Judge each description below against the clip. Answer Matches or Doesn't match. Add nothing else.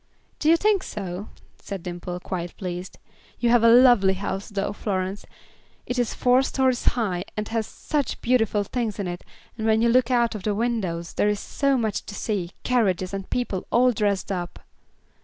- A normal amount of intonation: Matches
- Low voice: Doesn't match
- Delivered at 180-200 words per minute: Matches